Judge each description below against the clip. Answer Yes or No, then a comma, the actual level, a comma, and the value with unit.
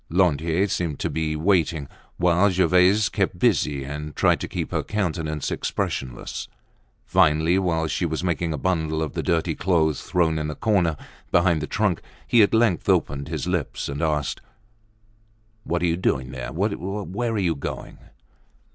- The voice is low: Yes, very low, 85 Hz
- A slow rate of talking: No, average, 165 wpm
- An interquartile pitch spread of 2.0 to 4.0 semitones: Yes, average, 3.2 semitones